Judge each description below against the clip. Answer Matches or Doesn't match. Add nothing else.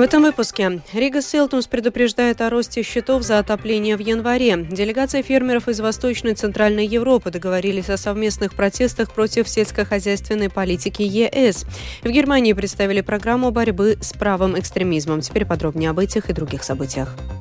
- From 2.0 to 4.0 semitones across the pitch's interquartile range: Matches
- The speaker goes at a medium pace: Matches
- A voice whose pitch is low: Doesn't match